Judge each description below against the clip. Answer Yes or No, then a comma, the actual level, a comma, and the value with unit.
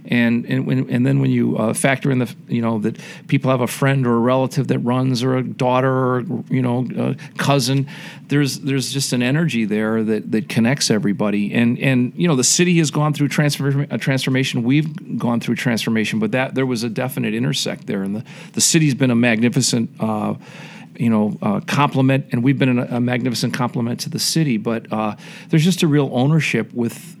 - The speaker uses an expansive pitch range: No, average, 3.1 semitones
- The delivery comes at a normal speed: No, fast, 210 wpm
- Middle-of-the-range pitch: No, low, 130 Hz